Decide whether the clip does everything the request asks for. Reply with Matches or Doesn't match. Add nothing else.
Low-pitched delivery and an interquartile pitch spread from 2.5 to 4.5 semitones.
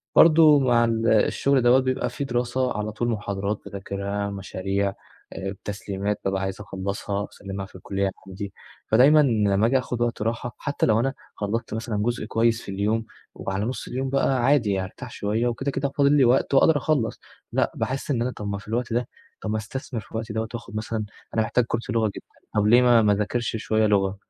Matches